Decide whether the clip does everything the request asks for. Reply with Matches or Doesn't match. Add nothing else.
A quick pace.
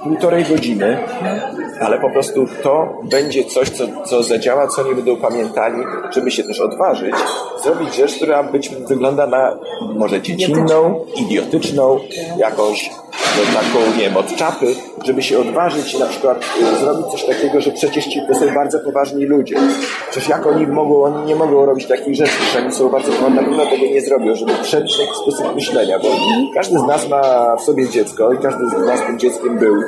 Matches